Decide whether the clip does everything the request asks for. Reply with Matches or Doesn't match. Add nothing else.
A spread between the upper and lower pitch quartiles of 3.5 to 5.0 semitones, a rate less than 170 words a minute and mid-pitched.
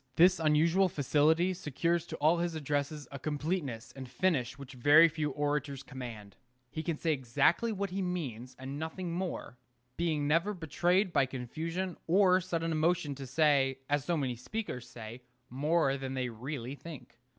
Matches